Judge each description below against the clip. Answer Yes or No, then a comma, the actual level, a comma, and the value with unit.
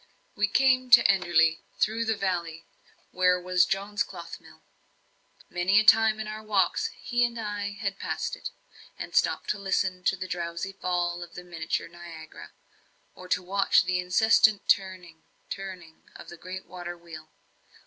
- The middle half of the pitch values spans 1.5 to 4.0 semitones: Yes, average, 2.9 semitones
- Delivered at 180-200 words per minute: No, average, 160 wpm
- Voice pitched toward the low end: No, medium, 185 Hz